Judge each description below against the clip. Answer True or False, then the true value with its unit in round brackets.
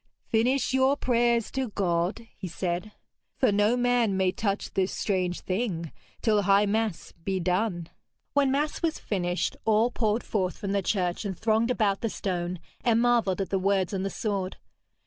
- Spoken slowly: False (170 wpm)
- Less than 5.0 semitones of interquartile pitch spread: True (3.9 semitones)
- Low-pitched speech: False (205 Hz)